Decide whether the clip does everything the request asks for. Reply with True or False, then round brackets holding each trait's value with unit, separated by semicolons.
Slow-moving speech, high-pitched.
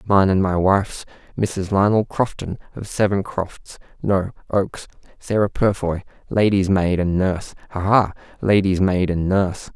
False (130 wpm; 95 Hz)